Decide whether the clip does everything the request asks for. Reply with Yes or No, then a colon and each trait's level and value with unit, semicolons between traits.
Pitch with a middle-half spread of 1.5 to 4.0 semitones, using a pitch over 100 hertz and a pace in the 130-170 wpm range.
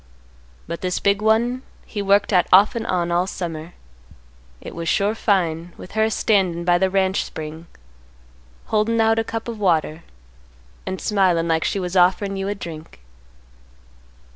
Yes: average, 3.6 semitones; high, 190 Hz; average, 165 wpm